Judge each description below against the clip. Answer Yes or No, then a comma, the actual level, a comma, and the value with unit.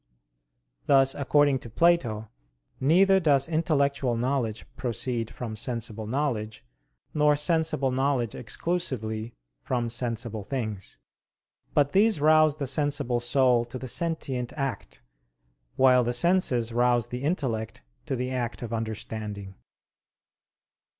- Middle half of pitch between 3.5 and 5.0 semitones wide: Yes, average, 4.0 semitones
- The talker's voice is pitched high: No, low, 125 Hz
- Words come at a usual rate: No, slow, 115 wpm